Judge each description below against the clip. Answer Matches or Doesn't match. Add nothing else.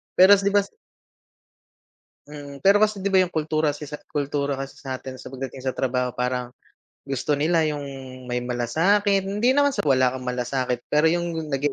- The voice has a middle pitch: Matches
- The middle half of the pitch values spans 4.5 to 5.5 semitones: Matches